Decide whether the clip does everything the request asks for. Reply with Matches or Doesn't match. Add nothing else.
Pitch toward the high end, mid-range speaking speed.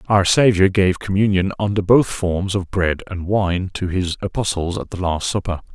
Doesn't match